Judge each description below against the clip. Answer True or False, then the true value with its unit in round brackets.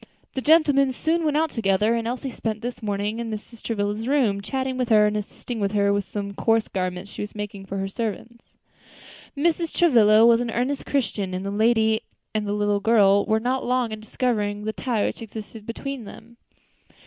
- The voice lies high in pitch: True (220 Hz)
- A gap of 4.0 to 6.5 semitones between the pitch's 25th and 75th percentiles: False (3.2 semitones)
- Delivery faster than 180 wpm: True (195 wpm)